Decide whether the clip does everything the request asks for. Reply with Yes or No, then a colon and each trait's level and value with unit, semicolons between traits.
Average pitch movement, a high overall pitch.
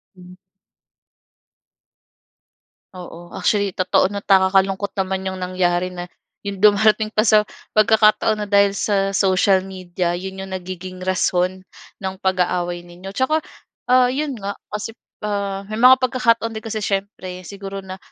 No: narrow, 2.3 semitones; high, 195 Hz